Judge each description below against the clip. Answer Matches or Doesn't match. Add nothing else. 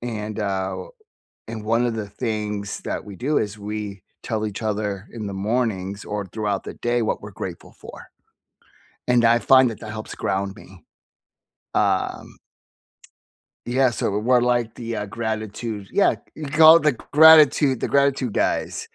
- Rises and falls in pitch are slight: Doesn't match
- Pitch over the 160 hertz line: Doesn't match